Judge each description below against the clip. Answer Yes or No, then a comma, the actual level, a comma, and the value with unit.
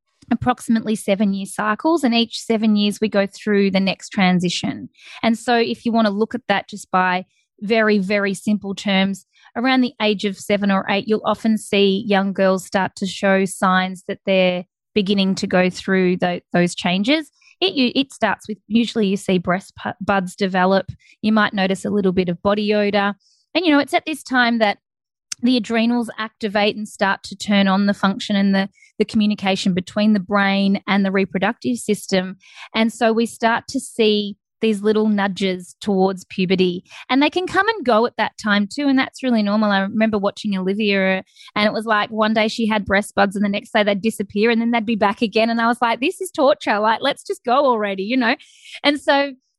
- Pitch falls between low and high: No, high, 210 Hz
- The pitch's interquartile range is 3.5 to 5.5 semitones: No, average, 3.0 semitones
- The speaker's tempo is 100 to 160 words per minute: No, fast, 205 wpm